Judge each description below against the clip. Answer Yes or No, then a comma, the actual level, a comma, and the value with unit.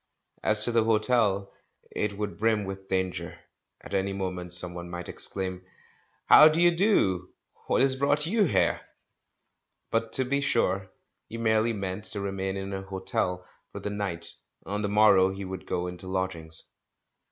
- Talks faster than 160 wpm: Yes, average, 170 wpm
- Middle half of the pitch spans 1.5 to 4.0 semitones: Yes, average, 3.3 semitones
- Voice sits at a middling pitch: No, low, 100 Hz